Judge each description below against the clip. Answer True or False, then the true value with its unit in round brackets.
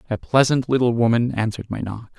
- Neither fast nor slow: True (190 wpm)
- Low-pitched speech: True (115 Hz)